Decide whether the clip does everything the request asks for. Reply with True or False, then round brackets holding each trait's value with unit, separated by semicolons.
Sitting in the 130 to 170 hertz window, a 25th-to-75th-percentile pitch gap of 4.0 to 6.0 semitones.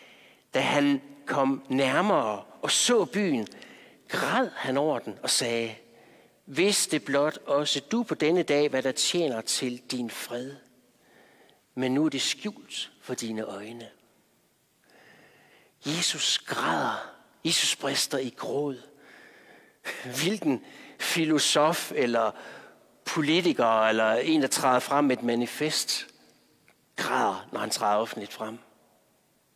False (135 Hz; 3.6 semitones)